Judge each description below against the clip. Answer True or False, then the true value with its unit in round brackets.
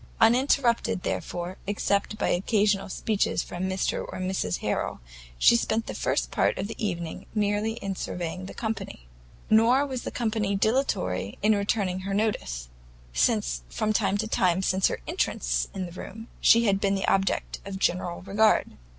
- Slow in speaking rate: False (160 wpm)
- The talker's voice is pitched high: True (200 Hz)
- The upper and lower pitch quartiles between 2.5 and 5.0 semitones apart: True (3.2 semitones)